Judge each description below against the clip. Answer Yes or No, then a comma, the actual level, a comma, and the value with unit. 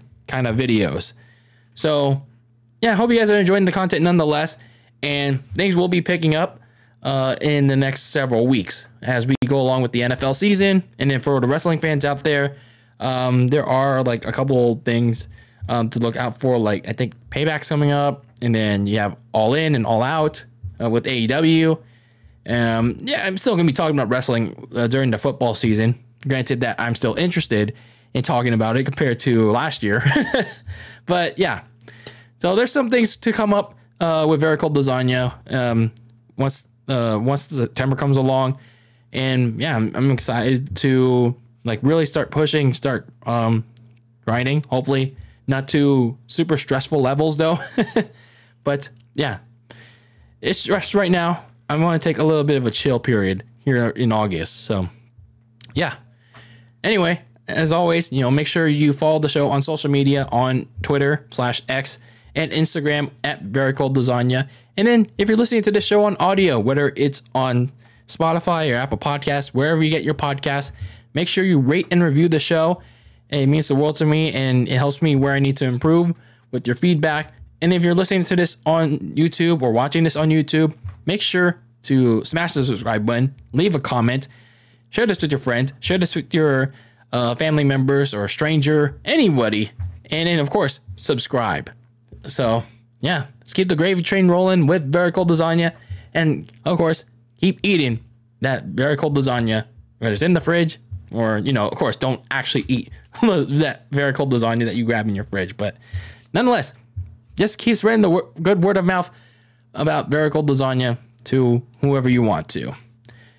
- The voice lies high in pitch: No, low, 135 Hz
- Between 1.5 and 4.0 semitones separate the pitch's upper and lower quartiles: No, average, 4.8 semitones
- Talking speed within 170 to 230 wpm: Yes, average, 180 wpm